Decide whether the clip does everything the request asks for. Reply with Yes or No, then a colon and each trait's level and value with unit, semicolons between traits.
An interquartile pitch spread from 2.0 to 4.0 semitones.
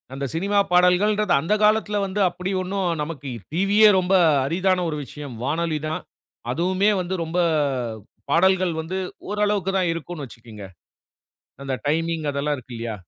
No: average, 4.4 semitones